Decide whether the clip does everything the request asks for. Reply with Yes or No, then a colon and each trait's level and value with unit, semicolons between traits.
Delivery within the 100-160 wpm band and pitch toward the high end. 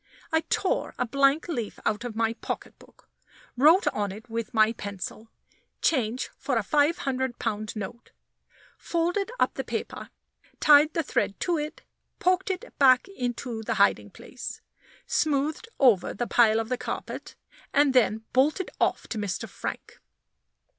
Yes: average, 150 wpm; very high, 255 Hz